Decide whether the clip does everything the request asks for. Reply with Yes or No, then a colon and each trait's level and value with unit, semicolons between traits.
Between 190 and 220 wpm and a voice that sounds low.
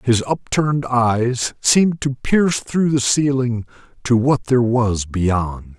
No: average, 145 wpm; low, 125 Hz